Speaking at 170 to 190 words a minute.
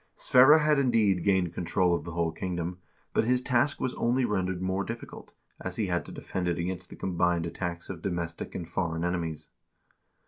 Yes: average, 185 wpm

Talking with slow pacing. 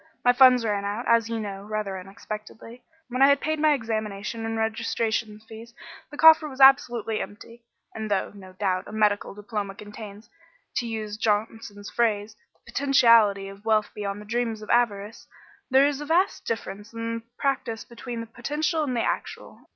No: average, 175 wpm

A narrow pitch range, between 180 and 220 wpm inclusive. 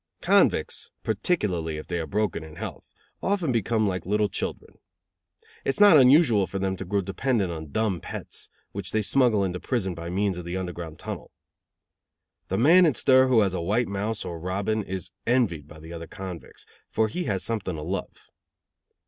No: average, 4.3 semitones; average, 185 wpm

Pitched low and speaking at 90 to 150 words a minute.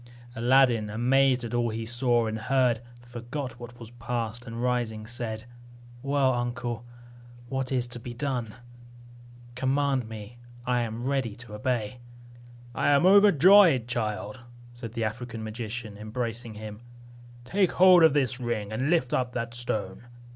Yes: low, 120 Hz; average, 145 wpm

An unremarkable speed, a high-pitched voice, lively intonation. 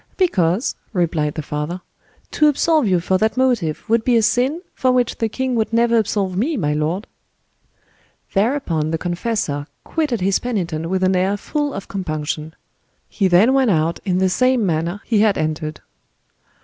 Yes: average, 170 wpm; high, 195 Hz; wide, 6.3 semitones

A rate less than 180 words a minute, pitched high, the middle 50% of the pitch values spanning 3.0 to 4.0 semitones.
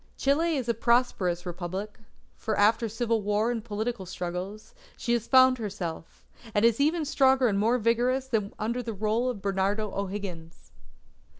Yes: average, 165 wpm; high, 220 Hz; average, 3.4 semitones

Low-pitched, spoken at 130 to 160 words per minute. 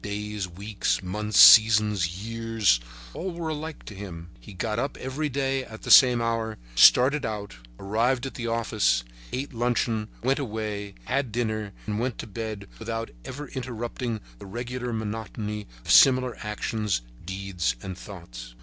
Yes: low, 110 Hz; average, 150 wpm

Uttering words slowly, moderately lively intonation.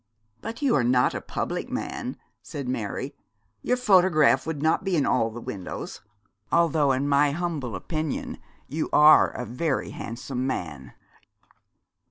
No: average, 145 wpm; average, 4.6 semitones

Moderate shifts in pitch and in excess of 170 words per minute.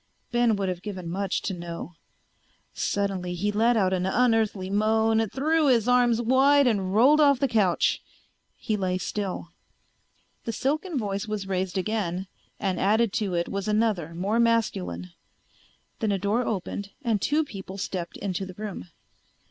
No: average, 3.7 semitones; average, 155 wpm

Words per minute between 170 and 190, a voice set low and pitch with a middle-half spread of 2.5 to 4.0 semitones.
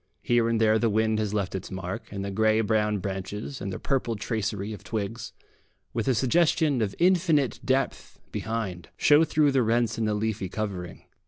Yes: average, 185 wpm; low, 110 Hz; average, 3.0 semitones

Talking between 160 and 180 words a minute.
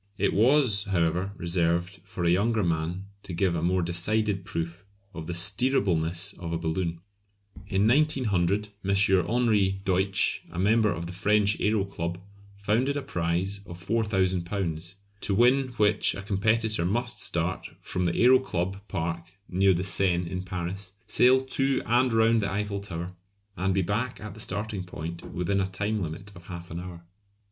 Yes: average, 165 wpm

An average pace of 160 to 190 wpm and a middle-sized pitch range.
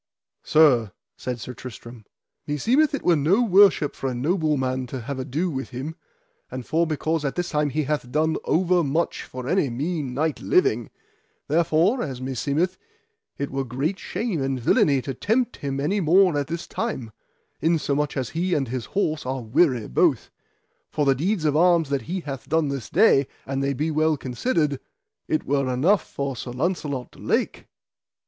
Yes: average, 180 wpm; average, 4.4 semitones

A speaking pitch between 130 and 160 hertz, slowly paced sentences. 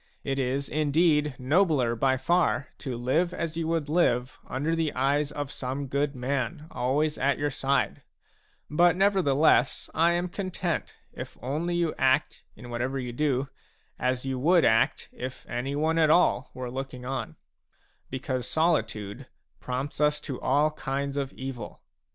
No: medium, 140 Hz; average, 155 wpm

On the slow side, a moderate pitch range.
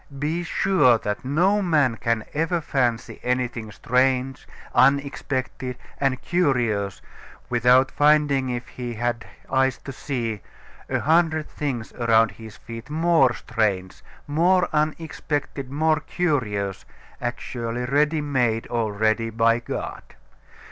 Yes: slow, 115 wpm; average, 4.5 semitones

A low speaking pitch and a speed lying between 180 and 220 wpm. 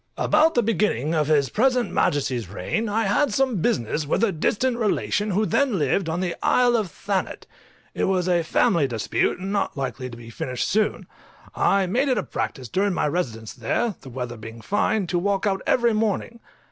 No: high, 190 Hz; average, 195 wpm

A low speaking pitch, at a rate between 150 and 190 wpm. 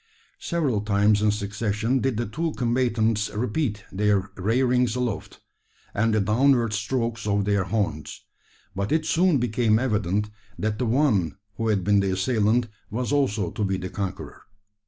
Yes: low, 110 Hz; average, 155 wpm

